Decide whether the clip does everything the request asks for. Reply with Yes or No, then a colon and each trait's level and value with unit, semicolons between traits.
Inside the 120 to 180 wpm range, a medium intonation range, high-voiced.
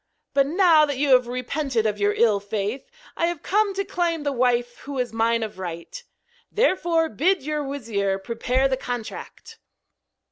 No: average, 170 wpm; wide, 6.0 semitones; very high, 260 Hz